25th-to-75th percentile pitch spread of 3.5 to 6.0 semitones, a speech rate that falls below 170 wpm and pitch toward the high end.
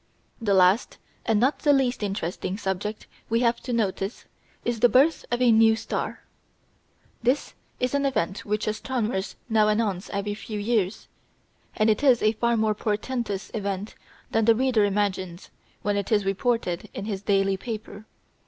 No: average, 2.9 semitones; average, 160 wpm; high, 215 Hz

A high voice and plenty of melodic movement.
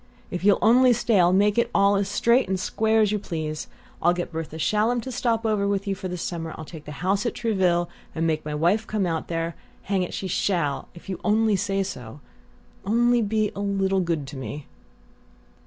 No: high, 195 Hz; average, 4.1 semitones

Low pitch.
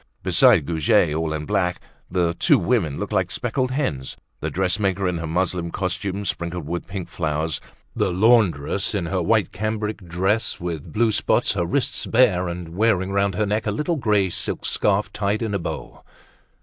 Yes: very low, 95 Hz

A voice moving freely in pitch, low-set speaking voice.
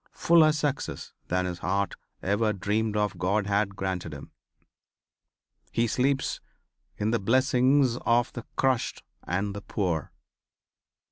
No: average, 4.5 semitones; low, 105 Hz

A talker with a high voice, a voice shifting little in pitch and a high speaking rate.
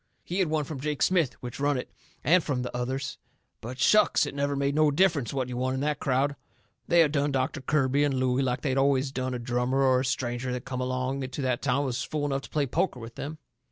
No: low, 135 Hz; narrow, 2.2 semitones; fast, 250 wpm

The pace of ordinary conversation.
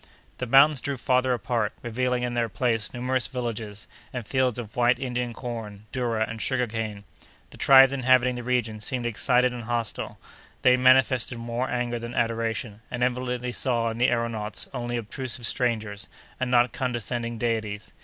Yes: average, 165 wpm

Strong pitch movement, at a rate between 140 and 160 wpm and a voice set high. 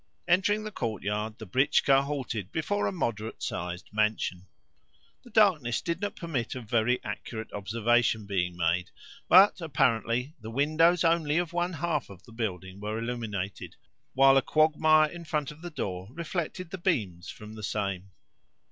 No: wide, 7.5 semitones; average, 155 wpm; low, 125 Hz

